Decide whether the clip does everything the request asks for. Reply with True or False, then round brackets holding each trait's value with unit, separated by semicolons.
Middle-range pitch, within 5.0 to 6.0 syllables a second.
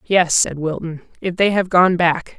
False (175 Hz; 4.3 syllables/s)